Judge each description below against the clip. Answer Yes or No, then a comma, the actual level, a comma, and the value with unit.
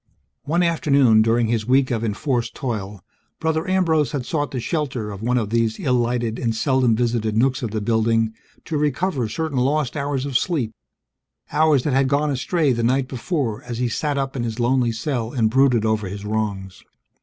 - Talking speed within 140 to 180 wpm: No, average, 190 wpm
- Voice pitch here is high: No, low, 125 Hz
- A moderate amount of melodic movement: Yes, average, 4.0 semitones